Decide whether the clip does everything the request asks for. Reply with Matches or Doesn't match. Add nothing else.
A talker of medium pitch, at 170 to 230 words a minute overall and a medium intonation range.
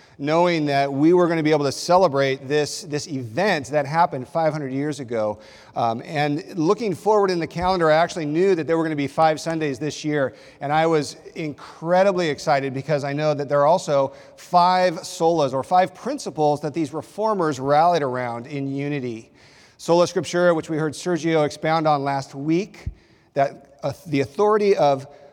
Matches